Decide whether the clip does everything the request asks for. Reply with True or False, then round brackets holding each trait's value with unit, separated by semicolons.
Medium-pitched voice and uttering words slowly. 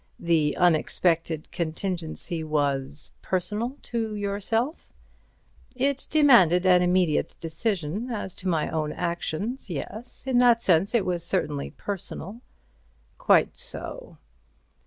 True (180 Hz; 105 wpm)